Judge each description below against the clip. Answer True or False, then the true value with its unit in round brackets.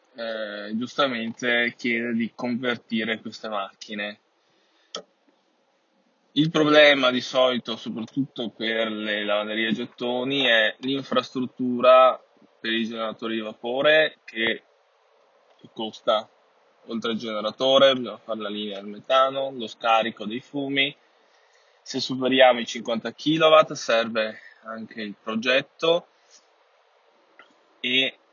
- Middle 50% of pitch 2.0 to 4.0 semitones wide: True (3.3 semitones)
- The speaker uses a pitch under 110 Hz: False (120 Hz)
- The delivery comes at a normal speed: False (105 wpm)